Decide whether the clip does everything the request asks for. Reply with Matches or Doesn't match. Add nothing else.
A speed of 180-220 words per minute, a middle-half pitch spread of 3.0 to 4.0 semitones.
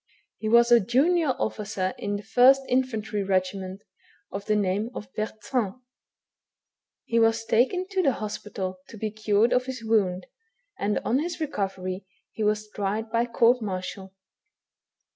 Doesn't match